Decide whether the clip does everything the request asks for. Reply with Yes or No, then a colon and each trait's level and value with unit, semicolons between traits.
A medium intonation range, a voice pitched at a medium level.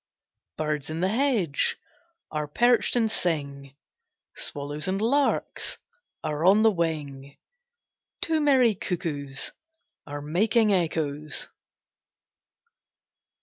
No: wide, 7.0 semitones; medium, 165 Hz